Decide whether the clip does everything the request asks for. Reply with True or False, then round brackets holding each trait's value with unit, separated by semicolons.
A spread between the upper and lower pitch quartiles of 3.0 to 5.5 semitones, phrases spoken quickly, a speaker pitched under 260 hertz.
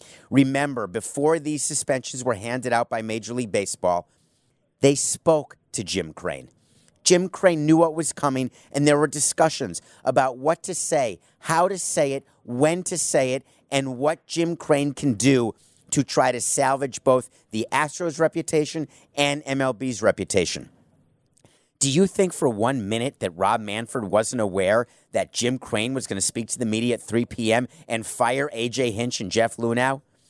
False (4.3 semitones; 170 wpm; 135 Hz)